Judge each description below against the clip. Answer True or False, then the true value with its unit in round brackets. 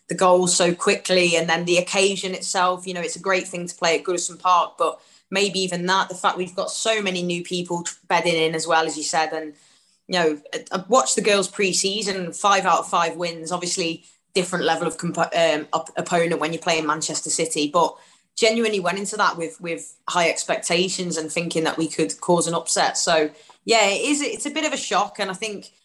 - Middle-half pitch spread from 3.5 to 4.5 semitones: False (2.8 semitones)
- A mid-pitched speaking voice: True (175 Hz)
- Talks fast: True (225 wpm)